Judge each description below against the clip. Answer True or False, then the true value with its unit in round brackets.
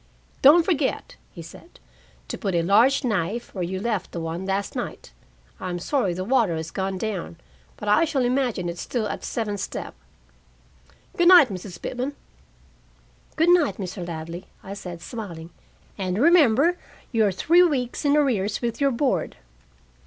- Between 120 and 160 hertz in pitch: False (210 Hz)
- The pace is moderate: True (165 wpm)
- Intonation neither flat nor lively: False (6.9 semitones)